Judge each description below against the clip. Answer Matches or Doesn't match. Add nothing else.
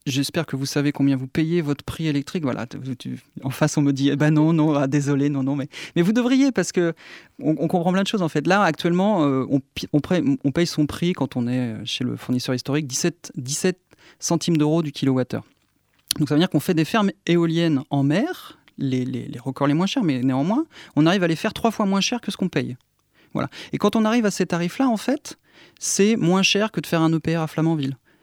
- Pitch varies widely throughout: Doesn't match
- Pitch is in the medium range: Matches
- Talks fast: Matches